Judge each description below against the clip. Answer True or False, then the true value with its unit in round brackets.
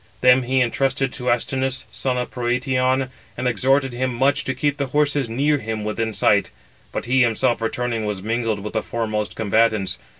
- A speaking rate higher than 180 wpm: False (175 wpm)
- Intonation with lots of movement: False (2.8 semitones)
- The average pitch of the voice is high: False (125 Hz)